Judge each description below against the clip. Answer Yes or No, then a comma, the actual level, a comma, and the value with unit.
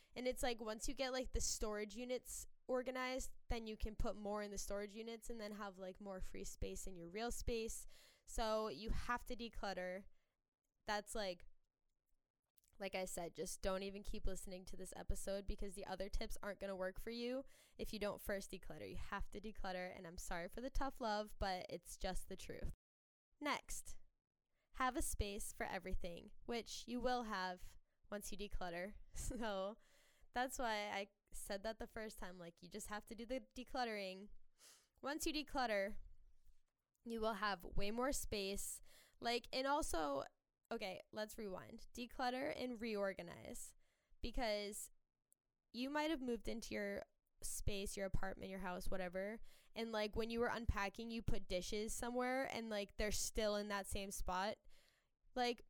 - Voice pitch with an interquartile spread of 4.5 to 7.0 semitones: No, average, 3.6 semitones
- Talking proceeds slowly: No, average, 170 wpm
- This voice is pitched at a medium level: No, high, 210 Hz